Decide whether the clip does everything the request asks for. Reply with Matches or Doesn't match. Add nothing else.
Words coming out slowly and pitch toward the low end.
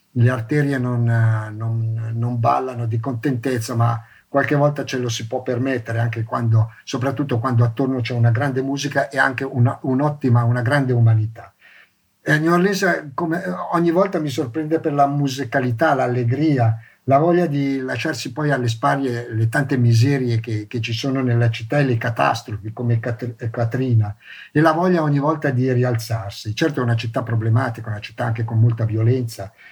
Doesn't match